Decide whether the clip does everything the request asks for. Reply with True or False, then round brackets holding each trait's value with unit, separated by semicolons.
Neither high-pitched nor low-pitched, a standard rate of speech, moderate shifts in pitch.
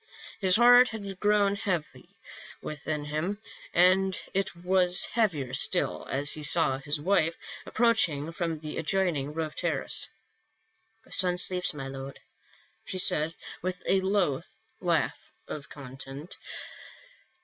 False (180 Hz; 125 wpm; 4.7 semitones)